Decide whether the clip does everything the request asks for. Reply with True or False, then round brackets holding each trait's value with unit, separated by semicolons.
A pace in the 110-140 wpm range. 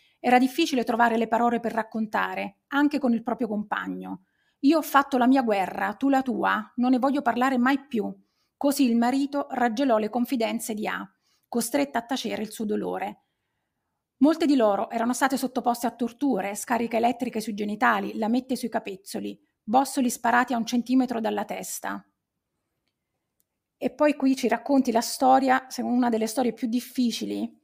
False (165 wpm)